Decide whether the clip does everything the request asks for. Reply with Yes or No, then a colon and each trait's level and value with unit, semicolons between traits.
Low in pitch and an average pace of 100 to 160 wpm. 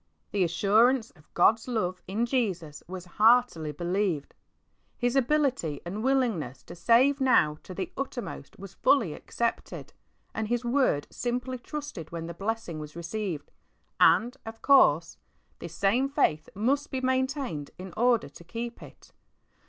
No: high, 220 Hz; average, 145 wpm